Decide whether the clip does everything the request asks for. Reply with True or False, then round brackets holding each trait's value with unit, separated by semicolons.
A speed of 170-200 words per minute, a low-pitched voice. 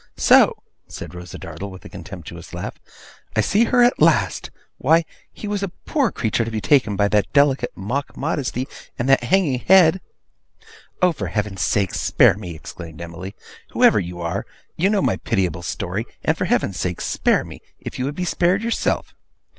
True (180 wpm; 115 Hz)